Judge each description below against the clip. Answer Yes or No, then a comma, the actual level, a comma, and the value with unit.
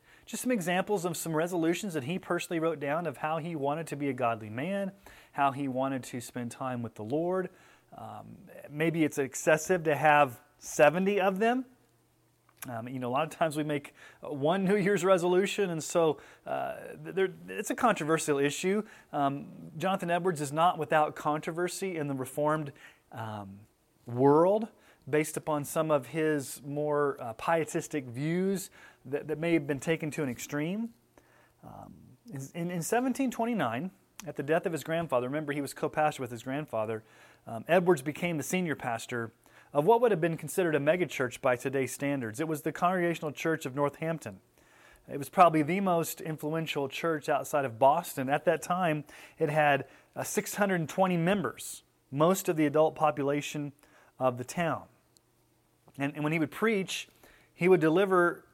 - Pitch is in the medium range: Yes, medium, 155 Hz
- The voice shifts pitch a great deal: No, average, 3.9 semitones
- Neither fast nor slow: Yes, average, 170 wpm